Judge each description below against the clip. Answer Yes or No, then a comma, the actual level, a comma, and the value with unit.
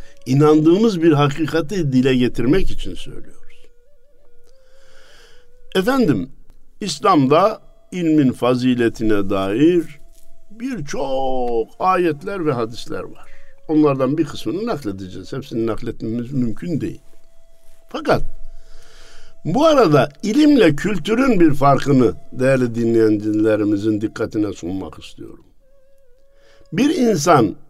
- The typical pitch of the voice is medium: Yes, medium, 150 Hz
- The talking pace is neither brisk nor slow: No, slow, 85 wpm